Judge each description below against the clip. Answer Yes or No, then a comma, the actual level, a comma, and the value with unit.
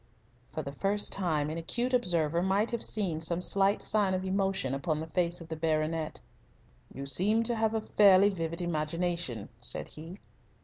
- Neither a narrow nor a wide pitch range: Yes, average, 3.9 semitones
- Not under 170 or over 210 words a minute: Yes, average, 175 wpm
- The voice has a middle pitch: Yes, medium, 175 Hz